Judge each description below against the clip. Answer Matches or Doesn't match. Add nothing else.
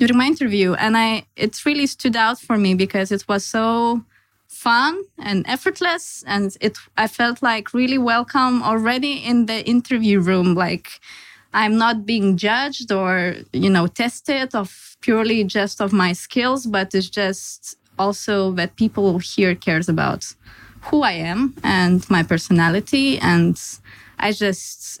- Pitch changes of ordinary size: Matches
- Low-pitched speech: Doesn't match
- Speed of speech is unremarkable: Matches